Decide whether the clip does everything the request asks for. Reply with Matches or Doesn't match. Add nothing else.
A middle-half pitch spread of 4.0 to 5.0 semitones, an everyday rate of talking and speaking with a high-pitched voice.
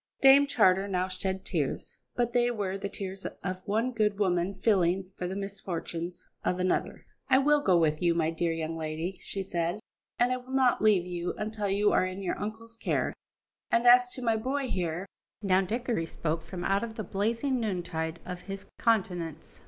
Matches